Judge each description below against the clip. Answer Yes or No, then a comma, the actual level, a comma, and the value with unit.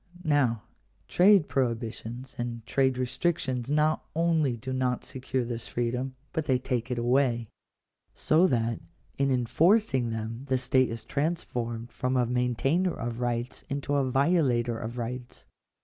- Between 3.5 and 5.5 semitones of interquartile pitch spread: No, average, 2.8 semitones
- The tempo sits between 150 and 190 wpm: No, average, 140 wpm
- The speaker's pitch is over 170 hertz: No, low, 125 Hz